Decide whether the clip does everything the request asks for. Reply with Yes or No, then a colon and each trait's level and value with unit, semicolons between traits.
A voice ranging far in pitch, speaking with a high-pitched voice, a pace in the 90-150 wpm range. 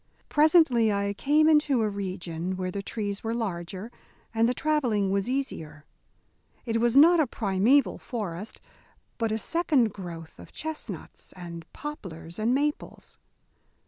Yes: wide, 6.6 semitones; high, 220 Hz; average, 140 wpm